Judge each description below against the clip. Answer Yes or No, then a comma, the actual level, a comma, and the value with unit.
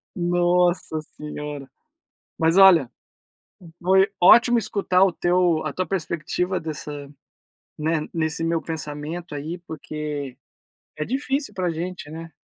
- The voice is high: No, medium, 165 Hz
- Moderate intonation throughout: Yes, average, 3.1 semitones